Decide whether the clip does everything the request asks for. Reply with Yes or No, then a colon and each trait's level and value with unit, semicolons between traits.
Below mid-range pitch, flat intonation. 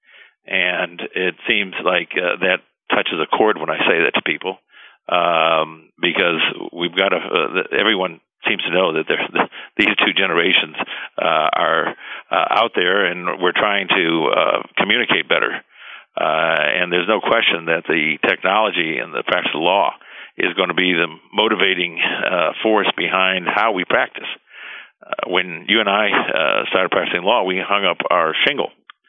Yes: very low, 90 Hz; narrow, 1.7 semitones